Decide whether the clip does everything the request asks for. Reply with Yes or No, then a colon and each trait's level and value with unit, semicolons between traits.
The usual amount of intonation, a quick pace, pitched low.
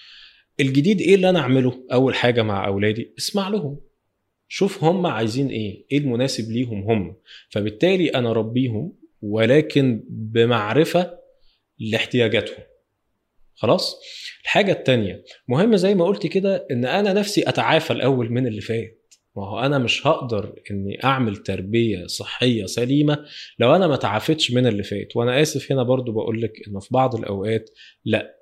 No: wide, 6.2 semitones; fast, 140 wpm; low, 125 Hz